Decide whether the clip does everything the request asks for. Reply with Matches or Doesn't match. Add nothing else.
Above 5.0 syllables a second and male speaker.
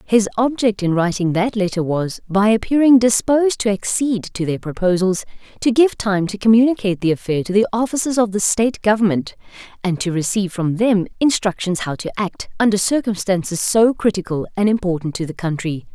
Doesn't match